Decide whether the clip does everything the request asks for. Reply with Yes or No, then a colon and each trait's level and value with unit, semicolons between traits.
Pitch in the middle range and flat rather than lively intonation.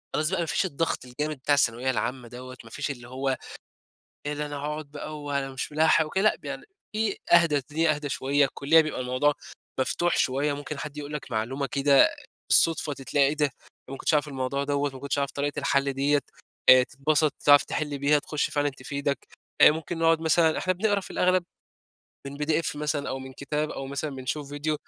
Yes: medium, 145 Hz; narrow, 2.0 semitones